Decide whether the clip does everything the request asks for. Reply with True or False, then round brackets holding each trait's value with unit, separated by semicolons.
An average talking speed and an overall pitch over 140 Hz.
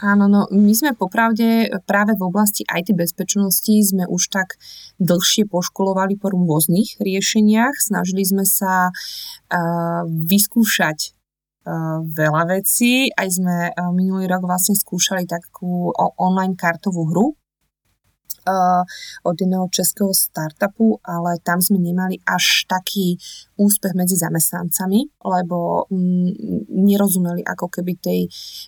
True (120 wpm; 185 Hz)